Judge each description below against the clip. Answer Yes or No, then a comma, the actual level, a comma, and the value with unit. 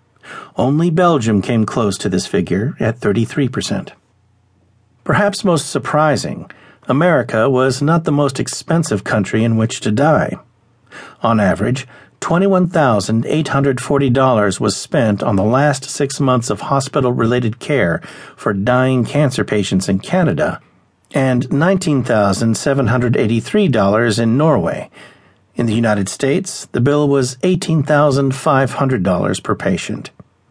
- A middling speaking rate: No, slow, 110 wpm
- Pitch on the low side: Yes, low, 130 Hz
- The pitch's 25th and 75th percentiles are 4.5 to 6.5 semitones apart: Yes, average, 4.8 semitones